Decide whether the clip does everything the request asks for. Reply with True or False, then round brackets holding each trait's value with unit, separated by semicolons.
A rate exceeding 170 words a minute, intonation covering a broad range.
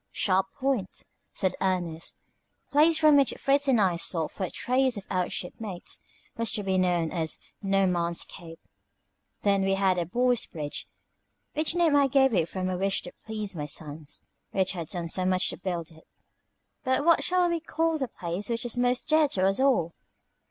True (195 wpm; 6.9 semitones)